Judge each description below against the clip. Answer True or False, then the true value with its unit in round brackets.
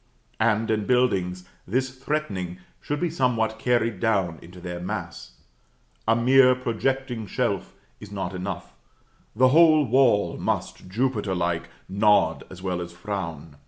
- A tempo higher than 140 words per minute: False (135 wpm)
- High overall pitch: False (110 Hz)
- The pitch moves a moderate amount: False (5.8 semitones)